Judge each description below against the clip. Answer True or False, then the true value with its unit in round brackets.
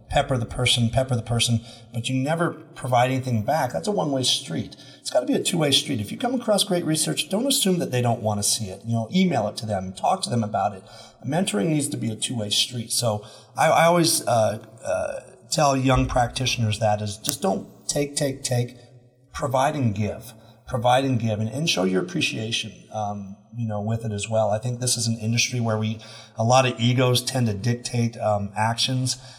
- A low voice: True (120 Hz)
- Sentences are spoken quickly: True (215 wpm)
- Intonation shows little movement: False (3.3 semitones)